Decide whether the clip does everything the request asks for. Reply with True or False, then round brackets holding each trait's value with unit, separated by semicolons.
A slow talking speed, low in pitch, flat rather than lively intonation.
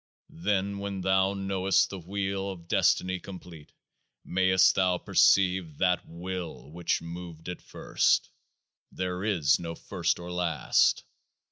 True (125 wpm; 95 Hz; 1.8 semitones)